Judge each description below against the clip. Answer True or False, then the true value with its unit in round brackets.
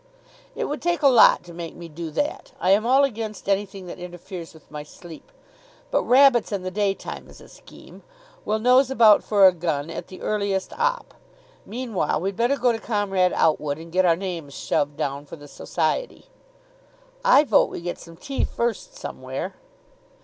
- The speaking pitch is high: True (195 Hz)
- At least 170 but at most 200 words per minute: True (185 wpm)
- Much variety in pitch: True (6.1 semitones)